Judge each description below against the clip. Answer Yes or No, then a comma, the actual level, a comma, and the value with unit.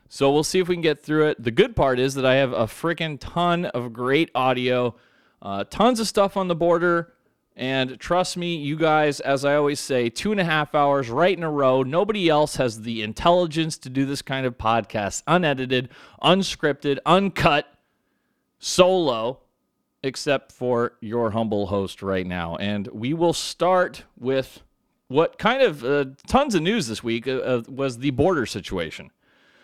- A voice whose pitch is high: No, medium, 140 Hz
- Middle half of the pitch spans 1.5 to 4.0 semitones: No, average, 5.3 semitones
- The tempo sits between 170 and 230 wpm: Yes, average, 180 wpm